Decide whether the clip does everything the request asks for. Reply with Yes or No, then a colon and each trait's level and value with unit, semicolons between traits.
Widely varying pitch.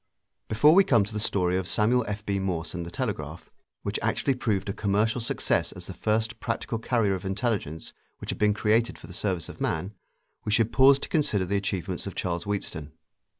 No: average, 3.5 semitones